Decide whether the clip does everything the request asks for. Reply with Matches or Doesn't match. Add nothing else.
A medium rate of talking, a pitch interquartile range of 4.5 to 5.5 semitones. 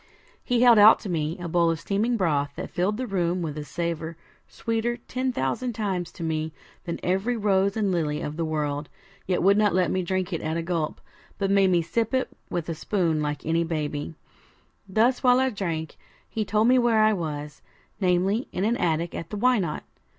Doesn't match